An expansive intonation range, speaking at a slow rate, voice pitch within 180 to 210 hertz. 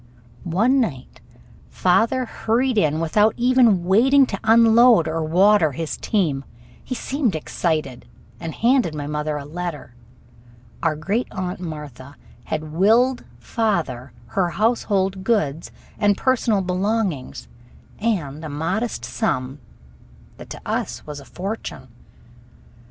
Yes: wide, 6.6 semitones; slow, 120 wpm; medium, 185 Hz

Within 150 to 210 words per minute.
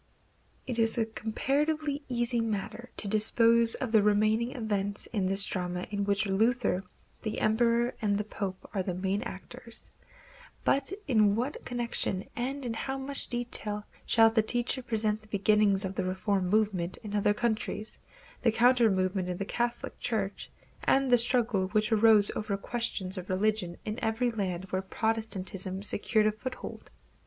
Yes: average, 160 wpm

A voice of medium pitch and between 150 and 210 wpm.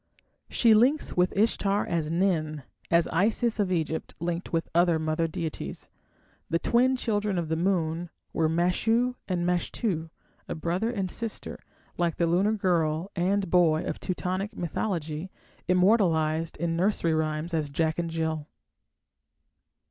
No: medium, 175 Hz; average, 140 wpm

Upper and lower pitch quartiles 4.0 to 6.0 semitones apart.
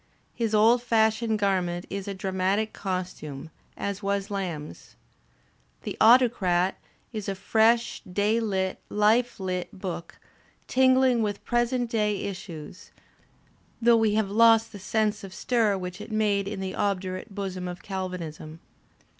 No: average, 3.0 semitones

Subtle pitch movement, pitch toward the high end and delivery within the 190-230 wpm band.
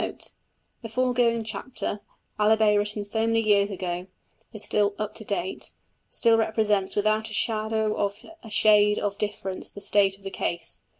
No: narrow, 1.5 semitones; high, 210 Hz; average, 165 wpm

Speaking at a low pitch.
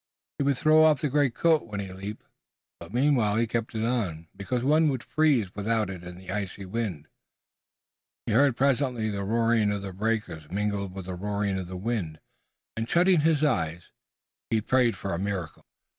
Yes: low, 110 Hz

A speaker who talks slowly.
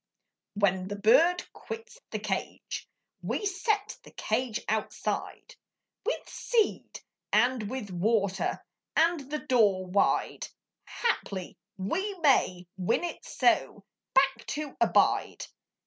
Yes: slow, 110 wpm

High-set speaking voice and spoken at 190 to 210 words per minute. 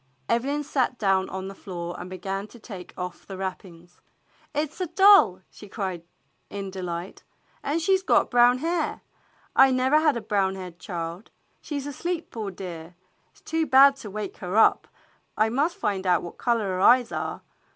Yes: high, 210 Hz; average, 195 wpm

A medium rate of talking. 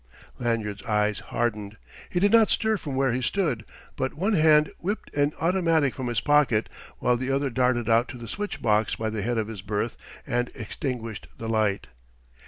Yes: average, 190 wpm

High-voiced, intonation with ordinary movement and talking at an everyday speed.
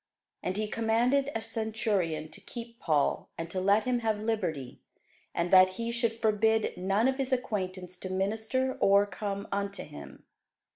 Yes: high, 210 Hz; average, 3.5 semitones; average, 160 wpm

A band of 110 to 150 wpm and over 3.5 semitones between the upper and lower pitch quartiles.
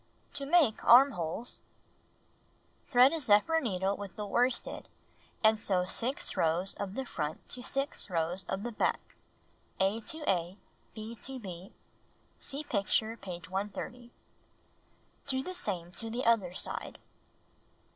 Yes: slow, 135 wpm; average, 5.1 semitones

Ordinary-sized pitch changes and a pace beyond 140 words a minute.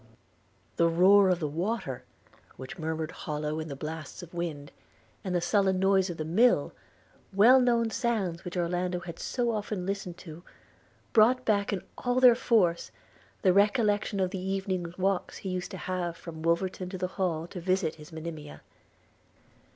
Yes: average, 3.2 semitones; average, 165 wpm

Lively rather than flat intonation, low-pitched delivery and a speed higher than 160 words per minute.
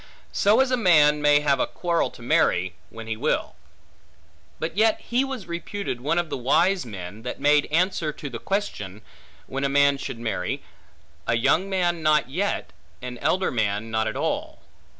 No: wide, 7.4 semitones; medium, 150 Hz; average, 180 wpm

